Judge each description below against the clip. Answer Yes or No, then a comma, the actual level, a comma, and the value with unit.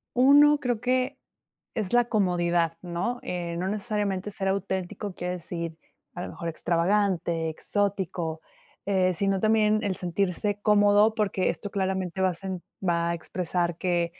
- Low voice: No, high, 190 Hz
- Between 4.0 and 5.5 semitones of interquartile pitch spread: No, average, 3.2 semitones